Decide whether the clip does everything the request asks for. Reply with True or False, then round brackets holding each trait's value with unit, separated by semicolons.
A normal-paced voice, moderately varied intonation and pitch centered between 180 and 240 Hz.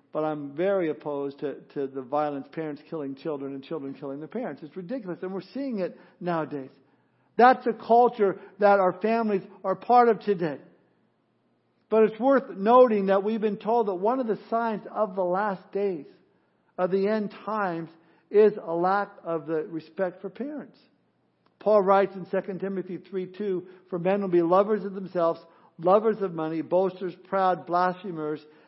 True (165 wpm; 3.9 semitones; 190 Hz)